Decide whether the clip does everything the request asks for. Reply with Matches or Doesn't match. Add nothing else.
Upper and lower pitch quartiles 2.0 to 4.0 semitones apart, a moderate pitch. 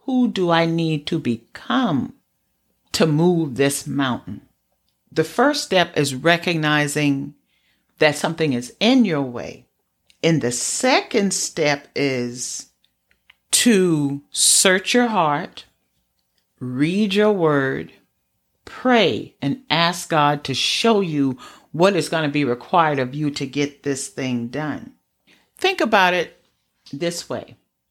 Doesn't match